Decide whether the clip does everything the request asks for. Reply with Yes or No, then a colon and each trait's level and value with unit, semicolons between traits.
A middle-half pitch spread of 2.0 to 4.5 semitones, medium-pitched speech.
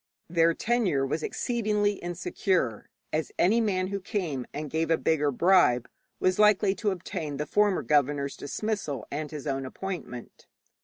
No: wide, 5.6 semitones; medium, 170 Hz